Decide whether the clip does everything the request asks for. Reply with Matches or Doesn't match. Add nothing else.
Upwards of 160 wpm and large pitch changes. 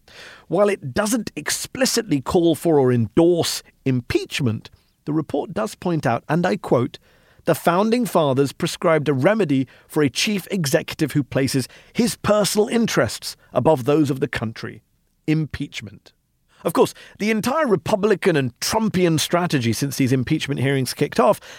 Doesn't match